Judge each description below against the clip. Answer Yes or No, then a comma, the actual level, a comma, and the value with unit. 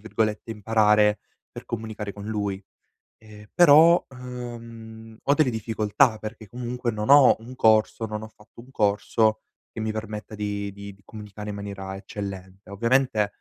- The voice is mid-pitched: No, low, 110 Hz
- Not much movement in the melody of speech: Yes, narrow, 2.1 semitones